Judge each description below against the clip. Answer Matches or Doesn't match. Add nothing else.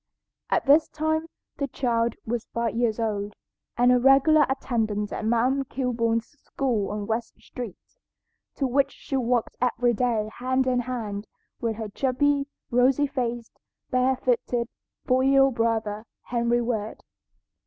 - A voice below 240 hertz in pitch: Doesn't match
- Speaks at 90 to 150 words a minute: Matches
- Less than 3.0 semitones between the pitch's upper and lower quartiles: Matches